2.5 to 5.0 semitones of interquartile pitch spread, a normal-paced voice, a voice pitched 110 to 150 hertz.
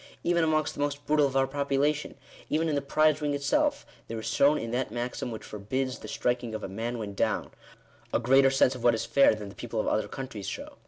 No: average, 4.0 semitones; fast, 245 wpm; low, 135 Hz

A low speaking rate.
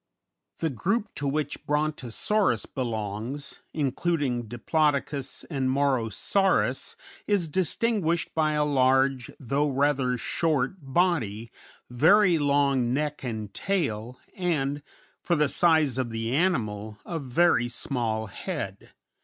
Yes: slow, 110 wpm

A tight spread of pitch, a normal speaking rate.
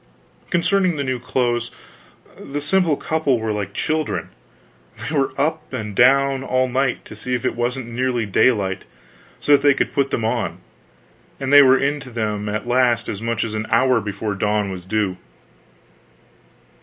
No: average, 4.2 semitones; average, 170 wpm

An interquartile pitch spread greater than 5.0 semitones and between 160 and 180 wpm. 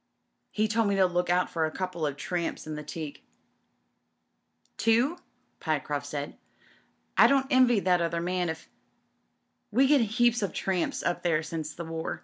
Yes: wide, 5.6 semitones; average, 170 wpm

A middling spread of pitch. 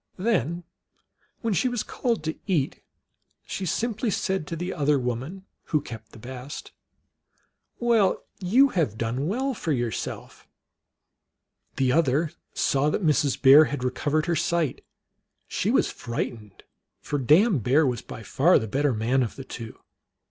No: wide, 6.4 semitones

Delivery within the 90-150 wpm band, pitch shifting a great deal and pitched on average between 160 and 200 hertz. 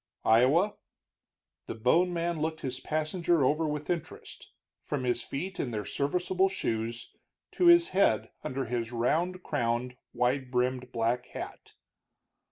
No: slow, 135 wpm; wide, 5.8 semitones; medium, 140 Hz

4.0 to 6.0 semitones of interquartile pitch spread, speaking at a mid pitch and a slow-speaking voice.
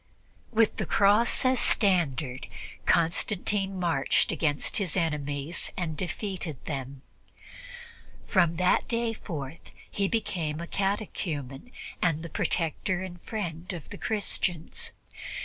Yes: average, 4.6 semitones; medium, 175 Hz; slow, 115 wpm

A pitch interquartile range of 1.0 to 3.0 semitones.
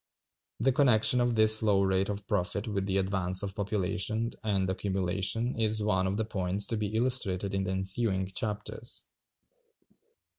Yes: narrow, 2.5 semitones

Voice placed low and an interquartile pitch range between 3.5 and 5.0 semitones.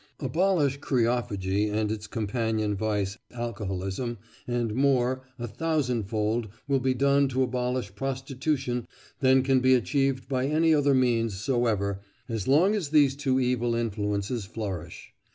Yes: low, 125 Hz; average, 3.9 semitones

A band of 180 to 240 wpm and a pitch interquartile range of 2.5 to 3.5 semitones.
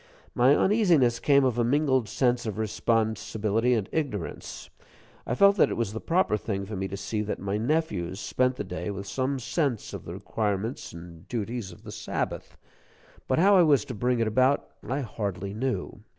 No: average, 190 wpm; average, 4.5 semitones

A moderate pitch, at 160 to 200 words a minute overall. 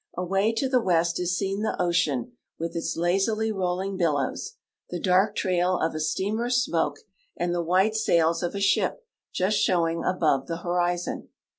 Yes: medium, 180 Hz; average, 165 wpm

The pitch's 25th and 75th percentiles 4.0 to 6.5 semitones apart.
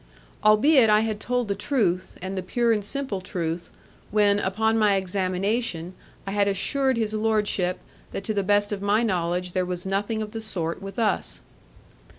No: average, 2.9 semitones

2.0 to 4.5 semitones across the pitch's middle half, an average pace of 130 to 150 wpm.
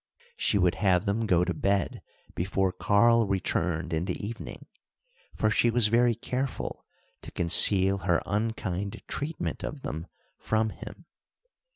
Yes: average, 4.0 semitones; average, 145 wpm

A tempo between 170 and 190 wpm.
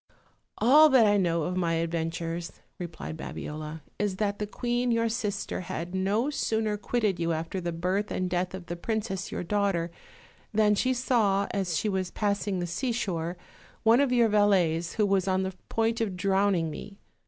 Yes: average, 175 wpm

